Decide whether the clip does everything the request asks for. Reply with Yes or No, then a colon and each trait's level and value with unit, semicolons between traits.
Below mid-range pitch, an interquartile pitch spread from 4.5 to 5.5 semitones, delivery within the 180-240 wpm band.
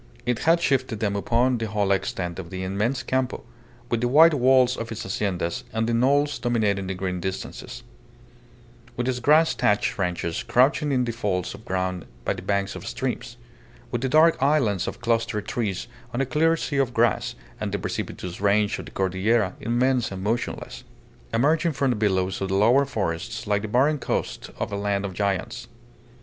Yes: low, 115 Hz; average, 4.8 semitones; average, 190 wpm